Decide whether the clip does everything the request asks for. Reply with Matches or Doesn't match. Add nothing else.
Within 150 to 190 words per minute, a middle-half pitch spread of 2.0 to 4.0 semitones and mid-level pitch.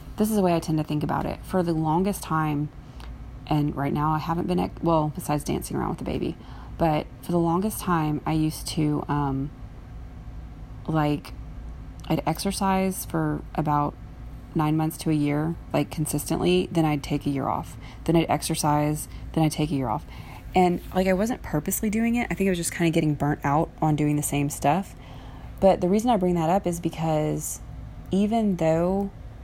Doesn't match